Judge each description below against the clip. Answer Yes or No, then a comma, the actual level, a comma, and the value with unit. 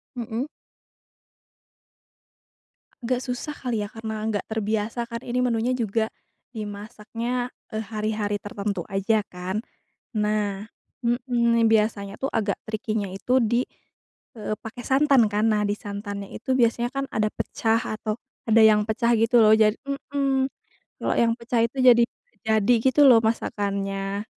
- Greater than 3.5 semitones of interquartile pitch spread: No, narrow, 2.4 semitones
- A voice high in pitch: Yes, high, 220 Hz